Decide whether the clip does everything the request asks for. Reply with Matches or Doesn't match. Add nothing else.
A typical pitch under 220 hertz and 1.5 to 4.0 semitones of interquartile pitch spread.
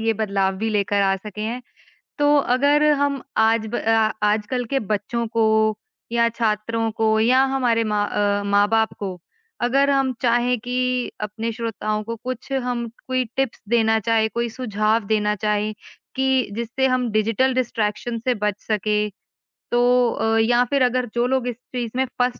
Doesn't match